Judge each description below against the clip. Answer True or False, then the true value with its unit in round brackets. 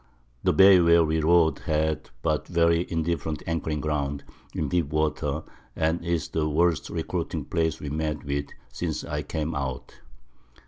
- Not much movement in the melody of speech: True (1.9 semitones)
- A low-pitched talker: True (80 Hz)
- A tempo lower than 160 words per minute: True (150 wpm)